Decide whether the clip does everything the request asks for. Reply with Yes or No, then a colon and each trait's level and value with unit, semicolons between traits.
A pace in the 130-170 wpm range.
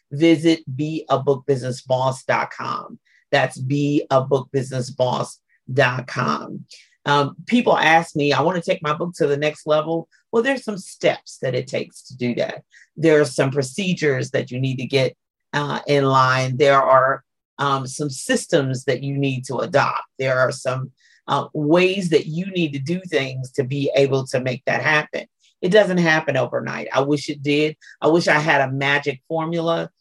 Yes: average, 165 wpm